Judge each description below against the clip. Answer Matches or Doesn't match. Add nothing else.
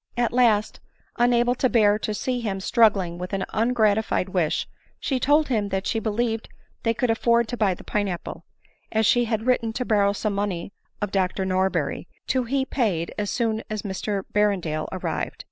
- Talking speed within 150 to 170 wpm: Doesn't match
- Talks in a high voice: Matches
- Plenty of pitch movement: Doesn't match